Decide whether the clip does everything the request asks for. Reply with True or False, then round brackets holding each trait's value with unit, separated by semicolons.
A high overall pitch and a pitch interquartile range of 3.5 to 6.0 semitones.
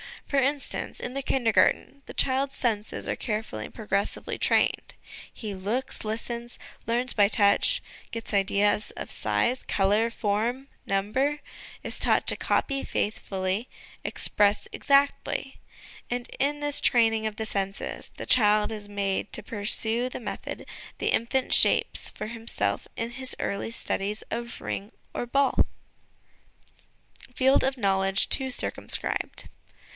True (225 Hz; 3.9 semitones)